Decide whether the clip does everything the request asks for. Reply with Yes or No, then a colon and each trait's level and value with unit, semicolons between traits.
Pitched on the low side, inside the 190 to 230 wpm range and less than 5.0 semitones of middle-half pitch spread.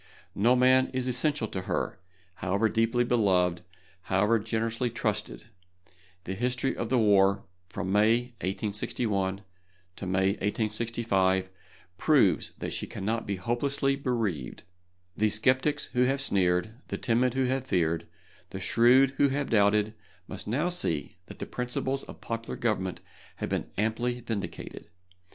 No: low, 115 Hz; average, 140 wpm; average, 4.1 semitones